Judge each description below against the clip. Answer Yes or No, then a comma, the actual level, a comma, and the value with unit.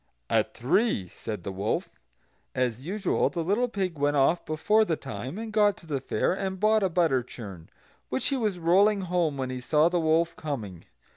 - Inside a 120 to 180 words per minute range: No, average, 195 wpm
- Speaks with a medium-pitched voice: Yes, medium, 165 Hz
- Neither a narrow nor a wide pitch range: No, wide, 7.2 semitones